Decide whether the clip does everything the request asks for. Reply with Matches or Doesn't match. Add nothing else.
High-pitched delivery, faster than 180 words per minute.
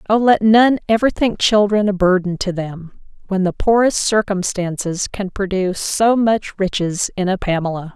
Doesn't match